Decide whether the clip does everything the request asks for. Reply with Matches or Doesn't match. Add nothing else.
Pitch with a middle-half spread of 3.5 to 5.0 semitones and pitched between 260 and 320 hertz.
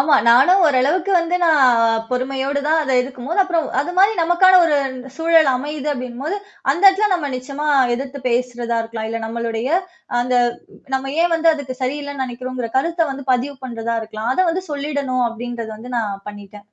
Matches